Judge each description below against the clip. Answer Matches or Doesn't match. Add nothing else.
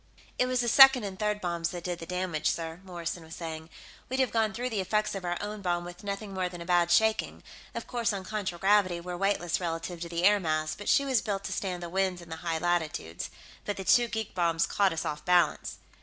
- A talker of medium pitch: Matches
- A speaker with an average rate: Doesn't match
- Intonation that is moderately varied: Matches